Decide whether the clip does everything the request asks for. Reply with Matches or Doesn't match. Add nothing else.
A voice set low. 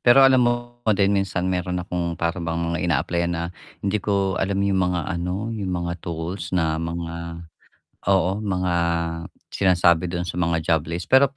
Matches